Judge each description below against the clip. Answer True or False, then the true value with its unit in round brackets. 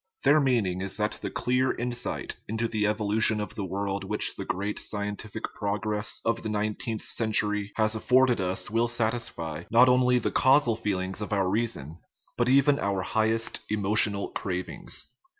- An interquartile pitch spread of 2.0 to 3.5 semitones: True (2.7 semitones)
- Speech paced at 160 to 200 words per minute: True (170 wpm)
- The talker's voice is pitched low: True (105 Hz)